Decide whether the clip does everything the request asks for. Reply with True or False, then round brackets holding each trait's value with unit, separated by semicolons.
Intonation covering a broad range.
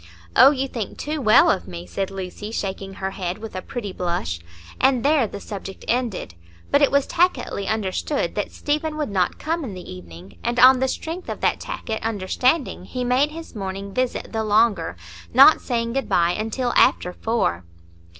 True (5.8 semitones)